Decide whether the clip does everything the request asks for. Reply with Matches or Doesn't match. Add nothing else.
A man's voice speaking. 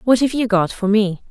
Doesn't match